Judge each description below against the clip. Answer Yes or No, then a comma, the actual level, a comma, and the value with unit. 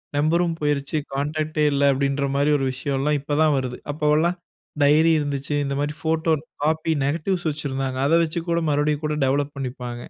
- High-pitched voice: No, medium, 145 Hz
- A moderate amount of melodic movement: No, narrow, 2.0 semitones